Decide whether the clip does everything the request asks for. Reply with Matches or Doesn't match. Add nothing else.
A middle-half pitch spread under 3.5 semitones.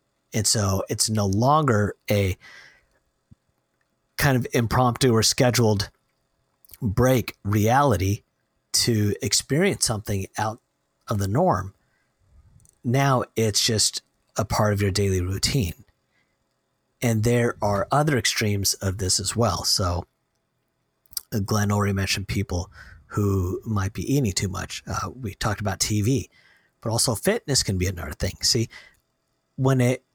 Doesn't match